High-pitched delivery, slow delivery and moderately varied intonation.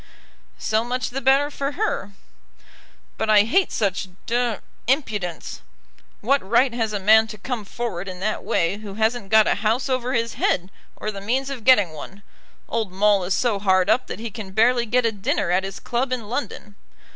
No: high, 220 Hz; average, 190 wpm; average, 3.8 semitones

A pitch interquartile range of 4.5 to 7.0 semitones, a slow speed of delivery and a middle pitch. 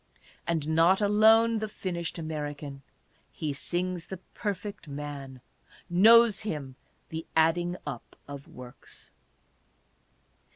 Yes: average, 5.3 semitones; slow, 115 wpm; medium, 165 Hz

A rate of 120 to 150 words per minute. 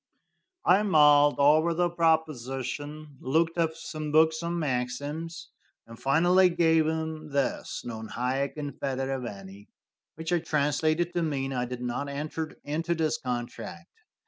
Yes: average, 140 wpm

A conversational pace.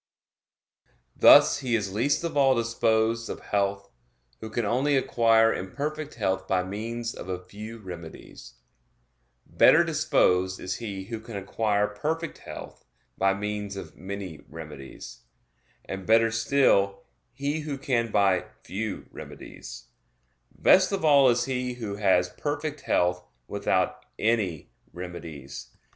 No: slow, 130 wpm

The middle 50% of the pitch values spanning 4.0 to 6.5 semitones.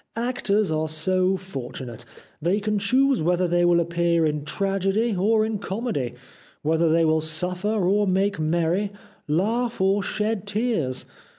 Yes: average, 4.5 semitones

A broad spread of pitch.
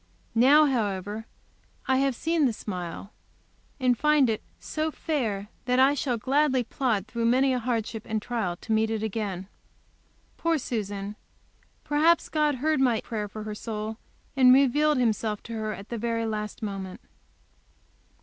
No: average, 4.0 semitones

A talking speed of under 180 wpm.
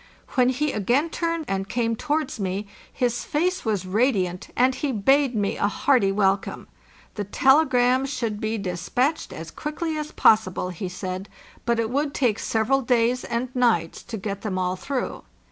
Yes: average, 170 wpm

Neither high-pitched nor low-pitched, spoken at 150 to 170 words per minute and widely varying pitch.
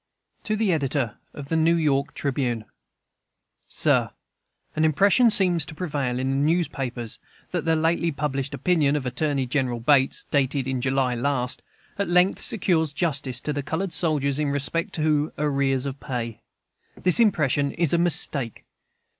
No: medium, 145 Hz; average, 155 wpm; average, 3.5 semitones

